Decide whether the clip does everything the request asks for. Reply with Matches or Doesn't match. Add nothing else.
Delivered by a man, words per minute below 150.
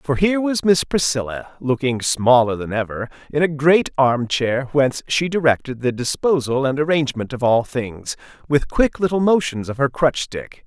Doesn't match